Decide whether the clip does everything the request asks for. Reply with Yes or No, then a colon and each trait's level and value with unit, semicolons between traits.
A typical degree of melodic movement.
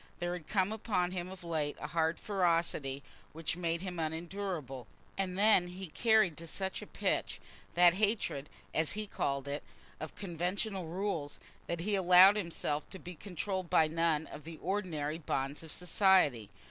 Yes: average, 3.3 semitones